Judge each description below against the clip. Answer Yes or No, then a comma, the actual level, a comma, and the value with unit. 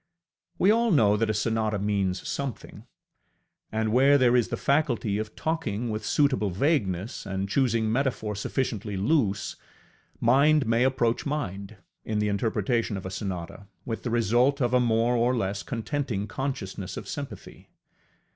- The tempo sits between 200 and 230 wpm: No, average, 150 wpm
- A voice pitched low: Yes, low, 115 Hz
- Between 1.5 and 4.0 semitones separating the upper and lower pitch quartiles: No, average, 4.4 semitones